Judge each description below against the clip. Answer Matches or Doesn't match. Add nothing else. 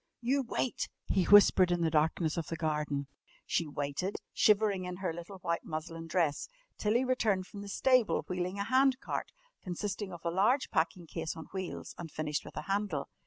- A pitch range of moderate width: Matches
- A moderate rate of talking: Matches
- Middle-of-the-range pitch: Matches